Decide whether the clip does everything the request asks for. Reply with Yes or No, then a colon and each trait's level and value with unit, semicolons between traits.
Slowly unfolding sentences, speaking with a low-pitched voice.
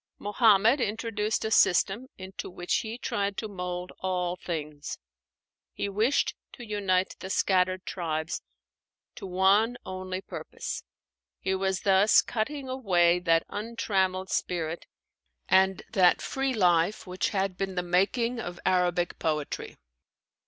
No: slow, 125 wpm; high, 190 Hz